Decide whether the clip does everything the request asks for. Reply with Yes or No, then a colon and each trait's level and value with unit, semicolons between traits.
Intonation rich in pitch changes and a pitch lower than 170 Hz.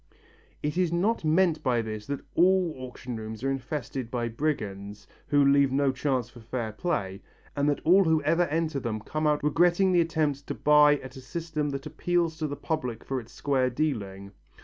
No: average, 4.6 semitones; medium, 140 Hz